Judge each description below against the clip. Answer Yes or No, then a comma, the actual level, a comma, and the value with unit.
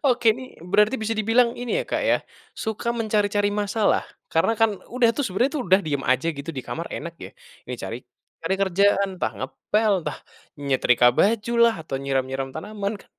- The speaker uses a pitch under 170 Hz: No, high, 205 Hz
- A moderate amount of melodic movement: No, wide, 7.2 semitones